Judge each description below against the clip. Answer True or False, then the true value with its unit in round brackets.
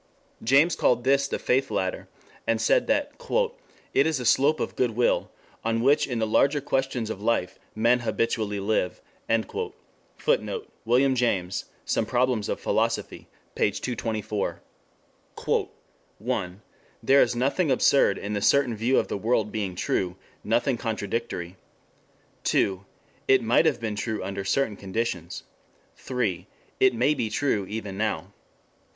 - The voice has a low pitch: True (115 Hz)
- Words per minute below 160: True (140 wpm)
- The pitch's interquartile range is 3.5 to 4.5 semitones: True (4.2 semitones)